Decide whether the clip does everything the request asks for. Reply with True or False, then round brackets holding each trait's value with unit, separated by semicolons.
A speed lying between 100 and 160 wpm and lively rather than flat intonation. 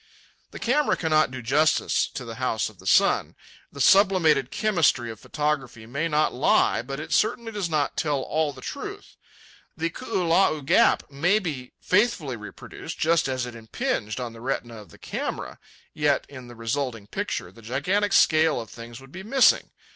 False (175 wpm; 6.0 semitones)